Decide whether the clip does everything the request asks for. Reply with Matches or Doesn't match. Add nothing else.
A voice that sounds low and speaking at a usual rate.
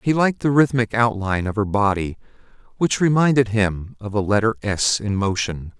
Matches